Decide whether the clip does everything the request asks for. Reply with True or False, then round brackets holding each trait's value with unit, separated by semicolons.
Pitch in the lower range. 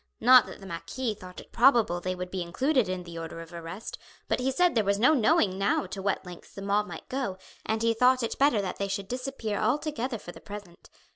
False (205 Hz)